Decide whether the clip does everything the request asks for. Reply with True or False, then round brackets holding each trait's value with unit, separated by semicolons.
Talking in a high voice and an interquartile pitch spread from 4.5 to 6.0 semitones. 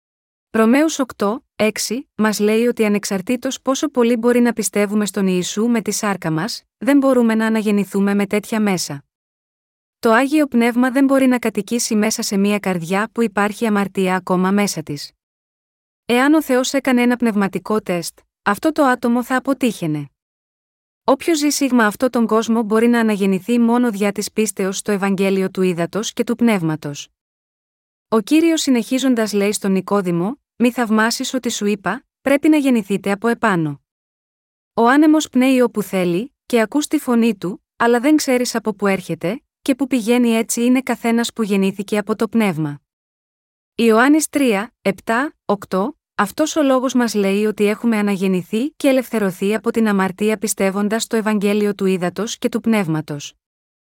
False (220 Hz; 3.7 semitones)